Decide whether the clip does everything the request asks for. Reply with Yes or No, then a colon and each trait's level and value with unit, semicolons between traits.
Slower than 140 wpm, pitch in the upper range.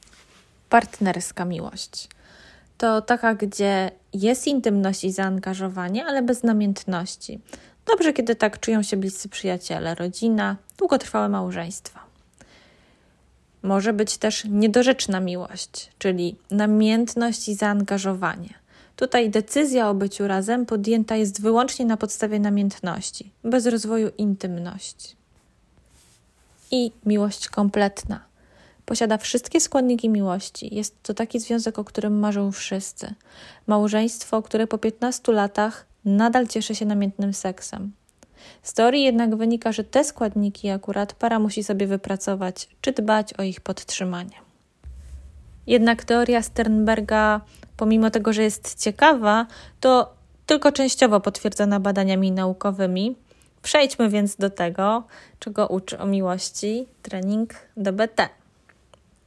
Yes: slow, 110 wpm; high, 210 Hz